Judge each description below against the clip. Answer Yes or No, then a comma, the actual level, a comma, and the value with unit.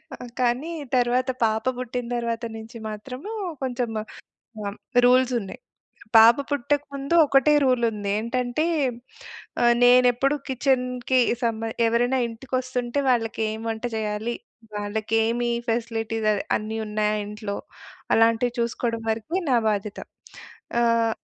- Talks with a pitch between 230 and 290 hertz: Yes, high, 235 Hz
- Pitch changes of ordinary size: No, narrow, 2.3 semitones